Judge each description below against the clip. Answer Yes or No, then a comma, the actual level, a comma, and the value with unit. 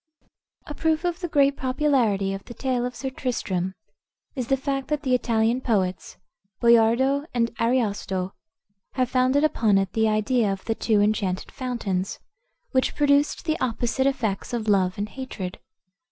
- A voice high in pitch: Yes, high, 240 Hz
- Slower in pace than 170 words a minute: Yes, average, 155 wpm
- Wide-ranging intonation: No, average, 4.7 semitones